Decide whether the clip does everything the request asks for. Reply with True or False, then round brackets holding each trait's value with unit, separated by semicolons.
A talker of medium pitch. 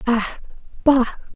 False (245 Hz)